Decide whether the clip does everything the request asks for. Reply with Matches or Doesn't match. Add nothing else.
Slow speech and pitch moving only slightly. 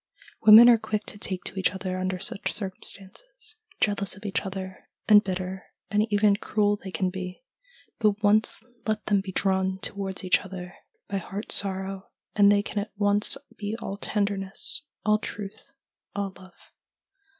Doesn't match